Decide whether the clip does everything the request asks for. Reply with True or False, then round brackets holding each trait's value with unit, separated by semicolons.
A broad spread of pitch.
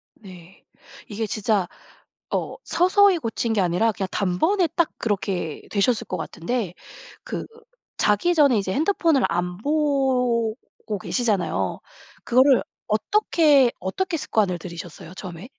True (7.1 semitones)